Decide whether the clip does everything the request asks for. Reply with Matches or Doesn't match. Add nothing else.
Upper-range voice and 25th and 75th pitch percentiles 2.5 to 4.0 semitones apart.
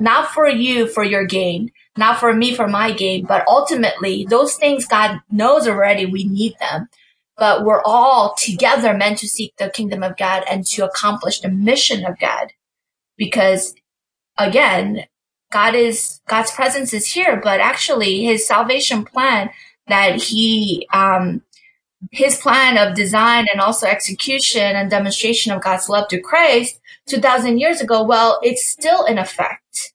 Doesn't match